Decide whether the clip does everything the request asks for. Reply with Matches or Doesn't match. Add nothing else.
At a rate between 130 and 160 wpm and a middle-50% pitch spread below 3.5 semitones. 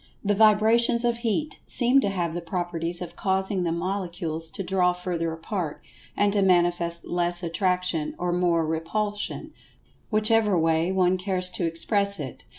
Matches